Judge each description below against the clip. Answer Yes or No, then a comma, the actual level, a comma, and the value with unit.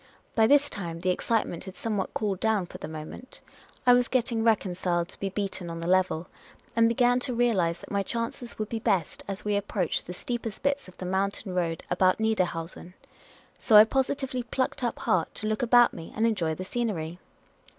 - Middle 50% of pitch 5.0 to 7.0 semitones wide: No, average, 4.4 semitones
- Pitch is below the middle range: No, high, 205 Hz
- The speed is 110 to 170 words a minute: No, average, 200 wpm